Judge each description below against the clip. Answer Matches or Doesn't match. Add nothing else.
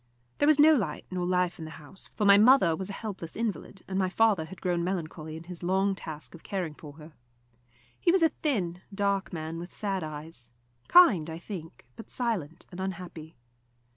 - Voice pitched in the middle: Matches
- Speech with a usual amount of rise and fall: Matches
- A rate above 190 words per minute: Matches